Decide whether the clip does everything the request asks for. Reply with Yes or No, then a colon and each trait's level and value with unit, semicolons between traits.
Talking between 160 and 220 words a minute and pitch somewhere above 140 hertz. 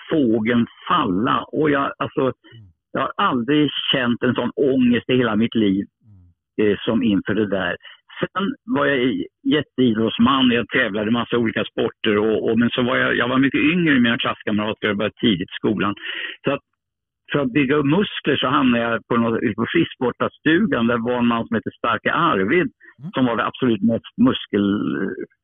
No: average, 180 wpm; low, 120 Hz